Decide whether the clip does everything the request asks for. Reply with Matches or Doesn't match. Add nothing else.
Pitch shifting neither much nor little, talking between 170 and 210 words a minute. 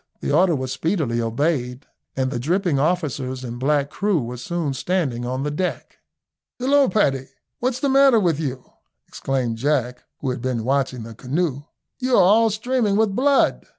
Doesn't match